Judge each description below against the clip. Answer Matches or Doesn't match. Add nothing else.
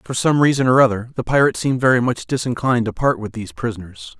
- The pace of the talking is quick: Matches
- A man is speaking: Matches